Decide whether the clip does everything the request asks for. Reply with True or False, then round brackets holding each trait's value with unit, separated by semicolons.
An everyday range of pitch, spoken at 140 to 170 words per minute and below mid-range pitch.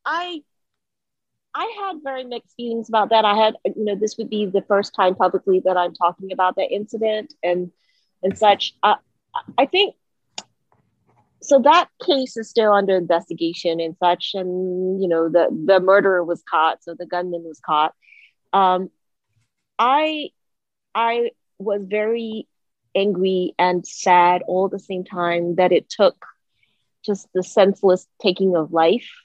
False (3.5 semitones; 155 wpm; 190 Hz)